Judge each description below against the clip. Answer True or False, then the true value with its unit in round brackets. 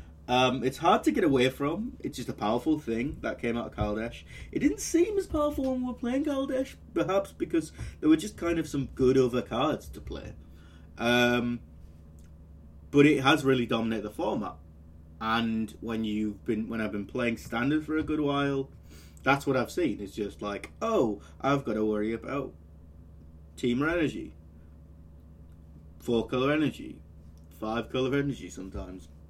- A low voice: True (115 Hz)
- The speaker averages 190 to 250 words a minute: False (170 wpm)